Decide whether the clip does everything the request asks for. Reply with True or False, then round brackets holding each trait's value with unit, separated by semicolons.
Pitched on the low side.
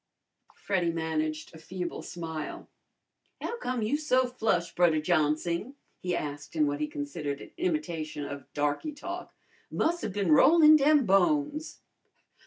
False (175 Hz)